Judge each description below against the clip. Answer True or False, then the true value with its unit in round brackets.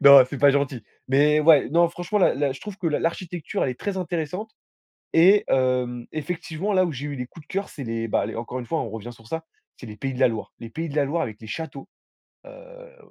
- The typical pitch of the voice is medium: True (145 Hz)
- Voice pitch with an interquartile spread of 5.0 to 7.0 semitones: True (5.4 semitones)